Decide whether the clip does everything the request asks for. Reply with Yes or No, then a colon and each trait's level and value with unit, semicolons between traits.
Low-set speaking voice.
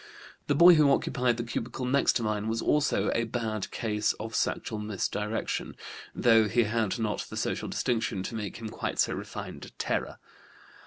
Yes: low, 115 Hz